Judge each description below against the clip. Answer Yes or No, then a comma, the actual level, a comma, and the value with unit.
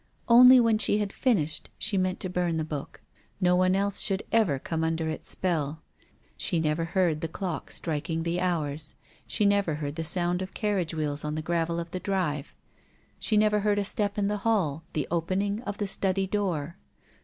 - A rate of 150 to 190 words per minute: No, average, 200 wpm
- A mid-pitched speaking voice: Yes, medium, 180 Hz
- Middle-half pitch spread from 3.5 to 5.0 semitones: Yes, average, 4.1 semitones